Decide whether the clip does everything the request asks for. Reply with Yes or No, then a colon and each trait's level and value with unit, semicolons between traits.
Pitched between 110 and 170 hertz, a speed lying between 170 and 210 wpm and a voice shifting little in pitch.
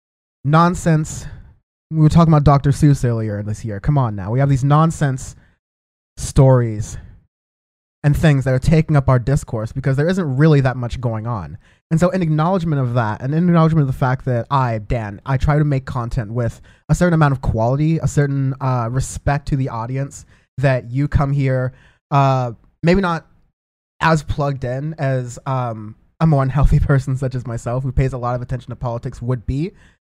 No: low, 135 Hz; average, 190 wpm; average, 3.5 semitones